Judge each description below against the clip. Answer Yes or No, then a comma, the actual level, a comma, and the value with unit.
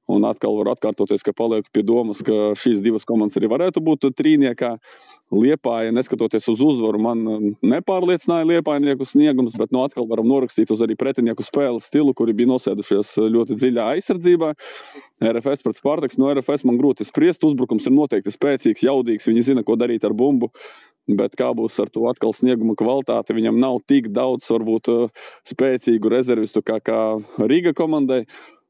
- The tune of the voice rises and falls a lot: No, average, 3.5 semitones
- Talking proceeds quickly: No, average, 165 wpm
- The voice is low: Yes, low, 120 Hz